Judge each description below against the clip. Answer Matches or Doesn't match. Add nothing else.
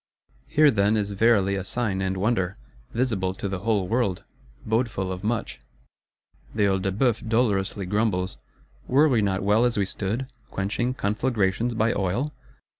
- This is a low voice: Matches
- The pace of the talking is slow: Doesn't match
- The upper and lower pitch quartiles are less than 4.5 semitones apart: Matches